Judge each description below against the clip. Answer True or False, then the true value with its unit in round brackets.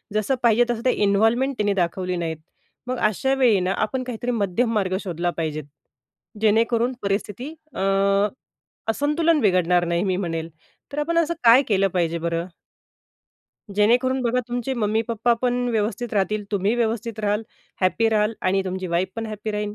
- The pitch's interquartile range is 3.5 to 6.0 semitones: True (4.4 semitones)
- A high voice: True (215 Hz)